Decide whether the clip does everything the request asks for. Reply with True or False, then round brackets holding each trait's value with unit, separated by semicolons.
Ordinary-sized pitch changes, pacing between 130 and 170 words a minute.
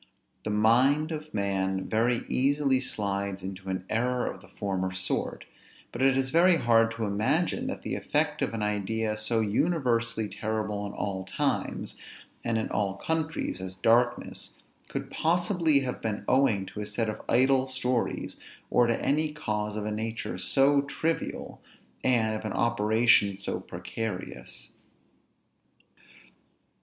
True (4.3 semitones; 145 wpm)